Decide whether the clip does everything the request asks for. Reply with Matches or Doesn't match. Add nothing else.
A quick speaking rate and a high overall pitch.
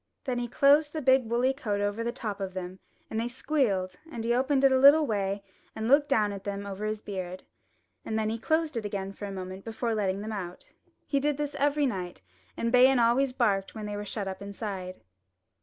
Matches